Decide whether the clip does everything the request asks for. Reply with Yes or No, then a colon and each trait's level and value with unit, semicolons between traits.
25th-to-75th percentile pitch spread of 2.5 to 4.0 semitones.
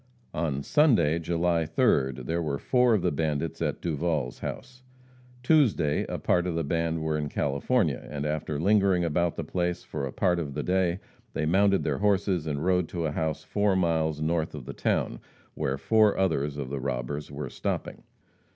Yes: average, 3.7 semitones